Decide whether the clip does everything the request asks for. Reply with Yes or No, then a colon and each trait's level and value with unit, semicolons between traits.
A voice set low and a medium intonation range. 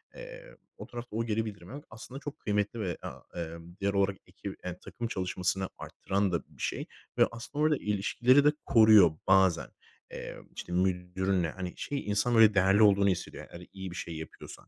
Yes: low, 100 Hz; average, 4.2 semitones